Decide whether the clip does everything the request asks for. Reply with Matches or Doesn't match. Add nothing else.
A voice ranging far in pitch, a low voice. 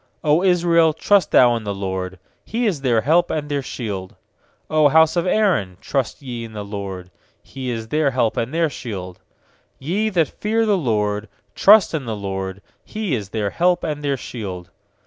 Matches